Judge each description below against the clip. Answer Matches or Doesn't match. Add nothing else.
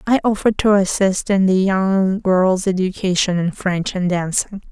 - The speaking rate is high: Doesn't match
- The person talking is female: Matches